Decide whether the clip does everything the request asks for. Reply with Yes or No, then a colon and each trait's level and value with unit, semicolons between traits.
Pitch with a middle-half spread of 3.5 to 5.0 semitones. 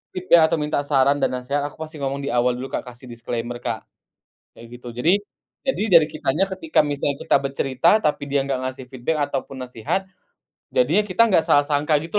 Yes: average, 3.8 semitones